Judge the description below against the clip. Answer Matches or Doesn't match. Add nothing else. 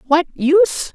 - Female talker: Matches